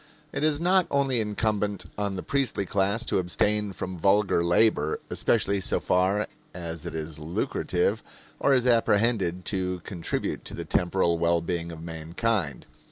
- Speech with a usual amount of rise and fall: Yes, average, 4.3 semitones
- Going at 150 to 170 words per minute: Yes, average, 155 wpm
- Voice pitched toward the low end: Yes, very low, 95 Hz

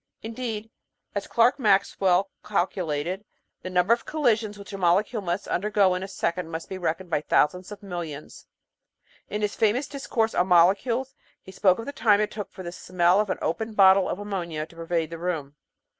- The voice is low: No, high, 190 Hz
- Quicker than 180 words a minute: Yes, average, 195 wpm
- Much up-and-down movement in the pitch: No, average, 3.4 semitones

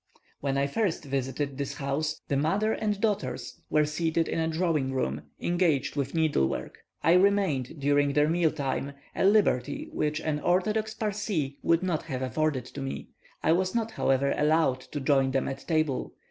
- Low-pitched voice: No, medium, 150 Hz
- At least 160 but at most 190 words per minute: Yes, average, 175 wpm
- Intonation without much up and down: No, average, 4.2 semitones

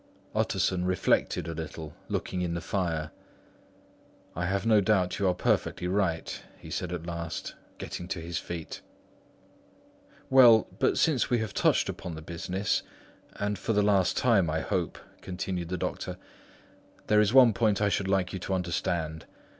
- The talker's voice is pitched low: Yes, very low, 90 Hz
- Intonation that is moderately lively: Yes, average, 3.3 semitones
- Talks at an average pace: Yes, average, 160 wpm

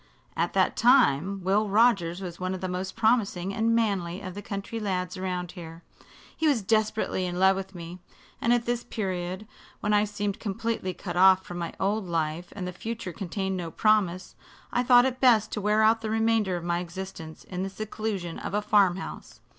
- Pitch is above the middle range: Yes, high, 195 Hz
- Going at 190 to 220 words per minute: Yes, average, 200 wpm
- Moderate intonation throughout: Yes, average, 3.2 semitones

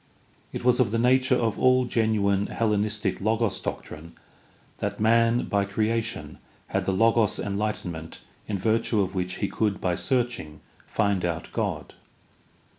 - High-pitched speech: No, low, 105 Hz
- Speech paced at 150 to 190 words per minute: No, average, 140 wpm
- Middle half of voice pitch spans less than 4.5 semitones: Yes, average, 2.8 semitones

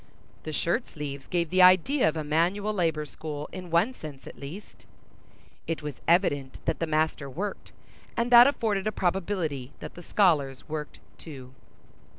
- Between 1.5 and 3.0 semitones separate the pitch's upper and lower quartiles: No, average, 4.5 semitones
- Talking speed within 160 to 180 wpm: Yes, average, 165 wpm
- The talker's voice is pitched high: No, medium, 165 Hz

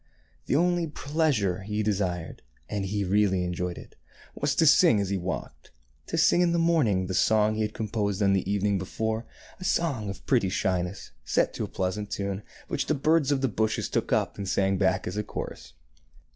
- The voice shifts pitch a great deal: Yes, wide, 6.0 semitones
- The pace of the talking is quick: Yes, fast, 210 wpm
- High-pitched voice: No, low, 105 Hz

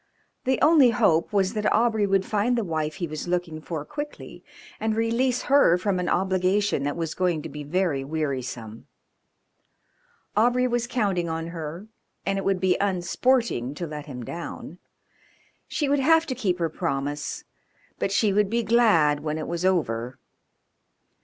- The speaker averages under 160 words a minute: No, average, 165 wpm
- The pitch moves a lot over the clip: Yes, wide, 6.0 semitones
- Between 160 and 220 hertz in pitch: Yes, medium, 185 Hz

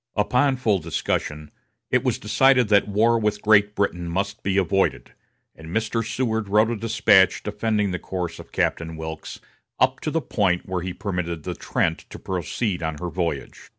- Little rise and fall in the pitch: No, average, 4.0 semitones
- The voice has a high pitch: No, low, 100 Hz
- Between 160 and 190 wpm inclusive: Yes, average, 175 wpm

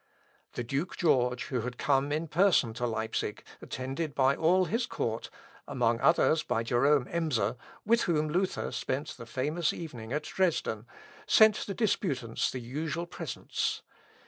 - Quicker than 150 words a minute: No, average, 145 wpm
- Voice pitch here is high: No, medium, 140 Hz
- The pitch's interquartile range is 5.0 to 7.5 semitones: Yes, wide, 5.5 semitones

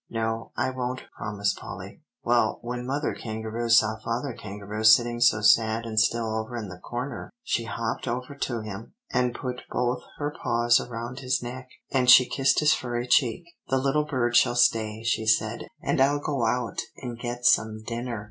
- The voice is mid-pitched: No, low, 120 Hz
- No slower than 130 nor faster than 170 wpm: No, average, 180 wpm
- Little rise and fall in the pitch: Yes, narrow, 2.2 semitones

